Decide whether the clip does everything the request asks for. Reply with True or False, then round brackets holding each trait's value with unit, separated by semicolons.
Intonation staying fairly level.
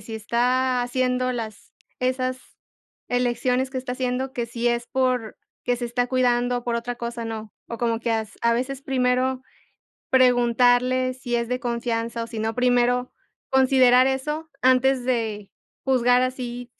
True (1.4 semitones)